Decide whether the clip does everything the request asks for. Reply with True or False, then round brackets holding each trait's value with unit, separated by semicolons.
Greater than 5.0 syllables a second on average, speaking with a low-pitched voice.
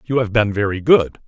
True (5.3 syllables/s; 110 Hz)